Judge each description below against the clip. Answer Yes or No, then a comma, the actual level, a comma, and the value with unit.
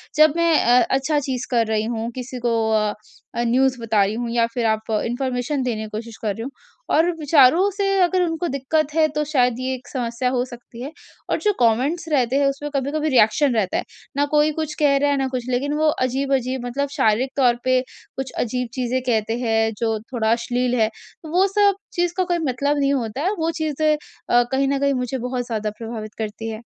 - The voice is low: No, very high, 255 Hz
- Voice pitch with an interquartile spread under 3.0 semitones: No, average, 3.7 semitones